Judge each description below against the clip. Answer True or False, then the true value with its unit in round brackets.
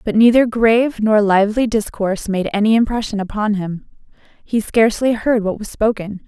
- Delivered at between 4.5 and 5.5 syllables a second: True (5.3 syllables/s)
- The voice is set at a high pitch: True (215 Hz)